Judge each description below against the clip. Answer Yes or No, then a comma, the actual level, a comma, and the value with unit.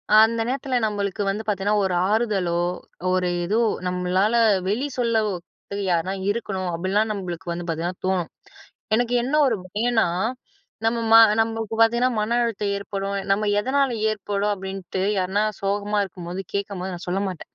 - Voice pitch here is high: Yes, high, 200 Hz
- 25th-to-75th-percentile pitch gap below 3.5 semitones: Yes, average, 3.1 semitones